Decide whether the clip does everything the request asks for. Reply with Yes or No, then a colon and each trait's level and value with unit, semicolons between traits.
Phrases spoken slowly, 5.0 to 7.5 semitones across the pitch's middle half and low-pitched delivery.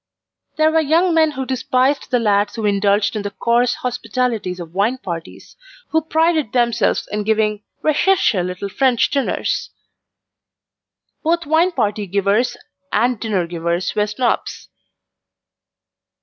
No: slow, 130 wpm; wide, 5.6 semitones; high, 230 Hz